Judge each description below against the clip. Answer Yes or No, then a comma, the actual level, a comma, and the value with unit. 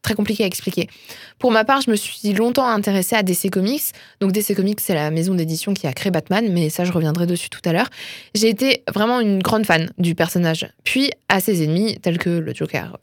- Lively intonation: No, average, 4.1 semitones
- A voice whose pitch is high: Yes, high, 195 Hz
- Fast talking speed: Yes, fast, 230 wpm